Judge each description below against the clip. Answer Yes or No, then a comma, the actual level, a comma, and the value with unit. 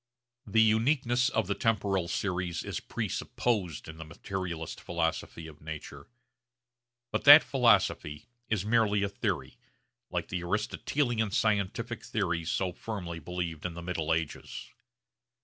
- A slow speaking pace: Yes, slow, 130 wpm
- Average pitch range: Yes, average, 4.9 semitones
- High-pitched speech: No, very low, 95 Hz